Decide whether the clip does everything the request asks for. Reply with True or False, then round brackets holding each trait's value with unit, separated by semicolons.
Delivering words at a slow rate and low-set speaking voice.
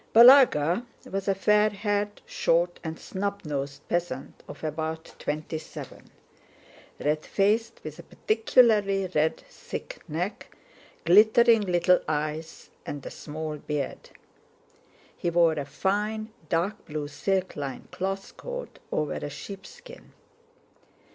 False (120 wpm; 180 Hz)